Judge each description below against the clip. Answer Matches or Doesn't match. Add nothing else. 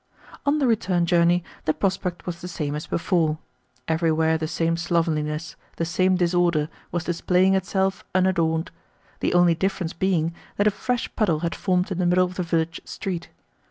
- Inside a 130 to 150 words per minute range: Doesn't match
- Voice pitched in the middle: Matches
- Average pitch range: Doesn't match